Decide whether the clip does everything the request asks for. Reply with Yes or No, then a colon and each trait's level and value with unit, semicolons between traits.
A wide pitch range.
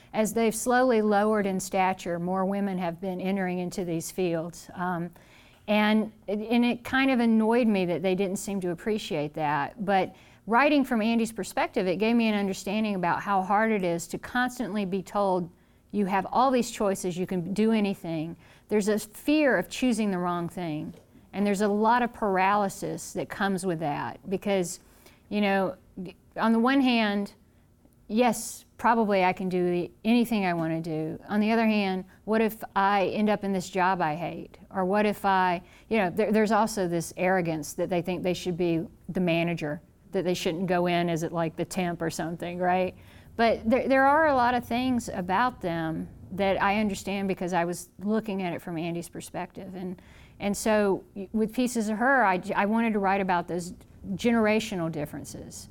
No: average, 3.4 semitones